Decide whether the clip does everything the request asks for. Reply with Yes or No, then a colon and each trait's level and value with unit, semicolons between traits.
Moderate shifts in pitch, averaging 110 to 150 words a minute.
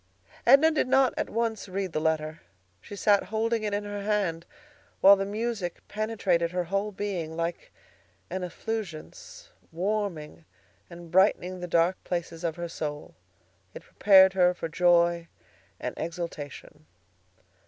Yes: average, 3.6 semitones; average, 140 wpm